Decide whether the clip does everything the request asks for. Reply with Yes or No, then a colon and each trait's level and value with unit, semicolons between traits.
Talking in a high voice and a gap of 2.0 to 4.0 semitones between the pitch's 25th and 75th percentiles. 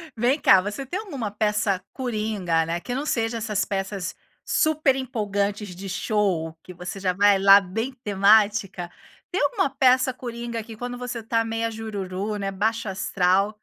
Yes: high, 210 Hz; average, 3.5 semitones